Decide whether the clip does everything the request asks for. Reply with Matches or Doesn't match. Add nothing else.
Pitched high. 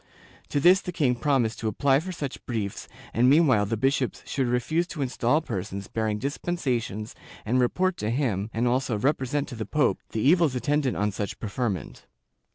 Doesn't match